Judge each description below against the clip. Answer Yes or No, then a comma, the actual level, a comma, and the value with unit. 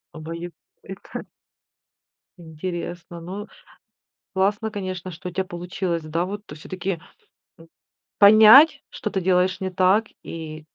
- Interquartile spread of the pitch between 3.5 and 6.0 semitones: No, narrow, 2.5 semitones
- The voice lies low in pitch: No, medium, 185 Hz